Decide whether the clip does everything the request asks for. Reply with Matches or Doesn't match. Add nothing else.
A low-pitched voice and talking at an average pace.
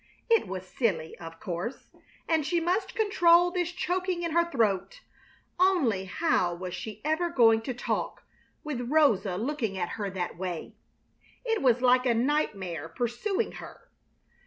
Doesn't match